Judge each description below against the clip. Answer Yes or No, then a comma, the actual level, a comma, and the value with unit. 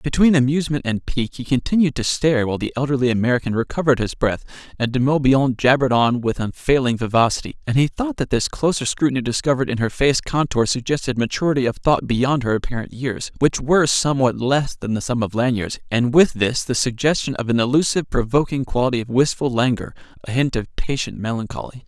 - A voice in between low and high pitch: No, low, 130 Hz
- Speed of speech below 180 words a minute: No, average, 185 wpm